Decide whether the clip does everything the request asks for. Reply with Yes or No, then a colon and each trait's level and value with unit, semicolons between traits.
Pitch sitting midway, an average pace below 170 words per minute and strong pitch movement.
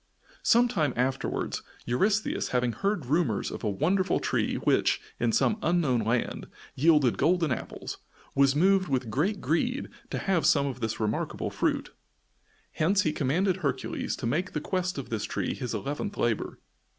Yes: medium, 150 Hz; average, 155 wpm; wide, 6.8 semitones